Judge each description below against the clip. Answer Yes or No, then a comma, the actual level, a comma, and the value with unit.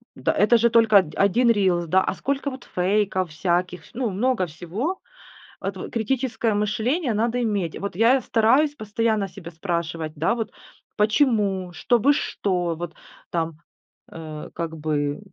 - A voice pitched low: No, high, 200 Hz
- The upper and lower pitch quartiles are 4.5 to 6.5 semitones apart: Yes, average, 5.2 semitones